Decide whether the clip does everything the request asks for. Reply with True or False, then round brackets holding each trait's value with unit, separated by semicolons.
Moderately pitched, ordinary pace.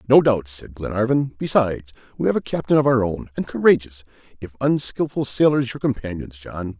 False (120 Hz; 175 wpm)